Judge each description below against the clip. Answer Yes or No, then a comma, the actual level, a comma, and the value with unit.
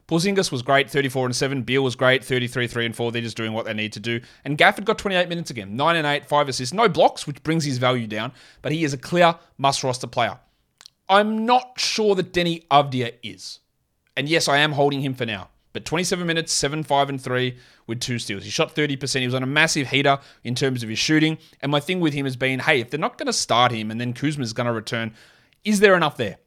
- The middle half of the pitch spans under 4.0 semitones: No, average, 4.4 semitones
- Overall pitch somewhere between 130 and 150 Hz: Yes, medium, 140 Hz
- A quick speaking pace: Yes, fast, 250 wpm